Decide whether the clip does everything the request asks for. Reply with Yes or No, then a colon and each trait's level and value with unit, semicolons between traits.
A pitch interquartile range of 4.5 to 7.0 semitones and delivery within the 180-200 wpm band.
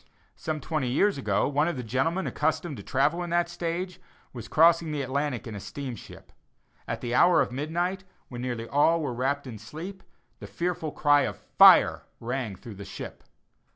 Yes: average, 5.0 semitones; average, 185 wpm